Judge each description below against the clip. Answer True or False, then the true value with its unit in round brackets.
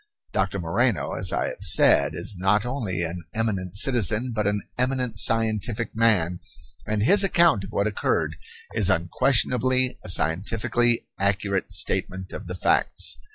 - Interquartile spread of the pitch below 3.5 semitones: False (4.6 semitones)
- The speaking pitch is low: True (105 Hz)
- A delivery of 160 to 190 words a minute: False (145 wpm)